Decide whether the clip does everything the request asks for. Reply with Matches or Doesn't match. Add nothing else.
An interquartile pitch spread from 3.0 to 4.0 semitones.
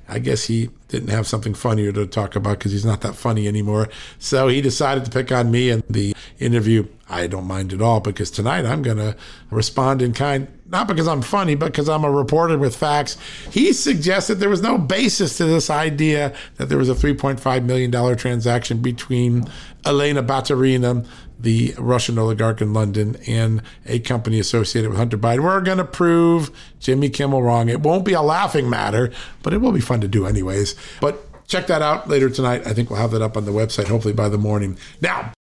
Doesn't match